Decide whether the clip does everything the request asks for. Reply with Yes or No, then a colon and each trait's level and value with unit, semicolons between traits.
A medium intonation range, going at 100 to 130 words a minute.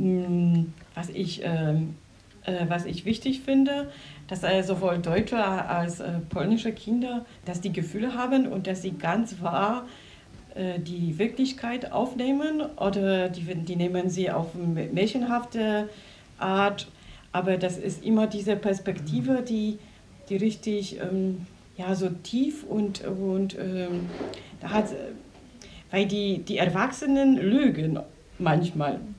Yes: average, 3.7 semitones; slow, 125 wpm